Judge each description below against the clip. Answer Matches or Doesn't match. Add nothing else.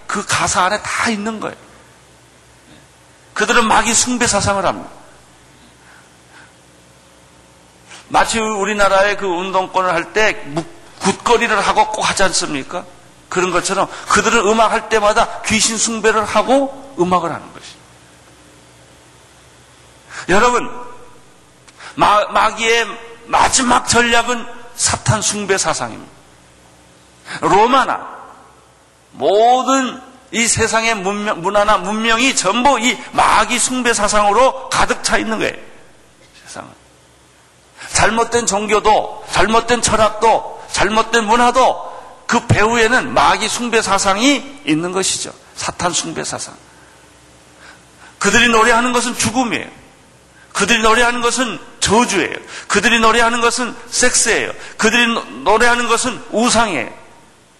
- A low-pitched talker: Doesn't match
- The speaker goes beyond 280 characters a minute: Doesn't match